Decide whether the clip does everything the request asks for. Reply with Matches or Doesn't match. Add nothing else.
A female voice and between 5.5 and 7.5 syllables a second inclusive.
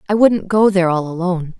Matches